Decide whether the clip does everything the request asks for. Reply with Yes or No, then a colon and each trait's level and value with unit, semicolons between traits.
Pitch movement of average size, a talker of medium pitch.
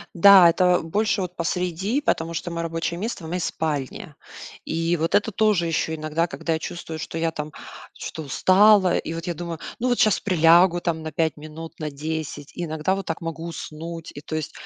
No: narrow, 2.2 semitones; medium, 165 Hz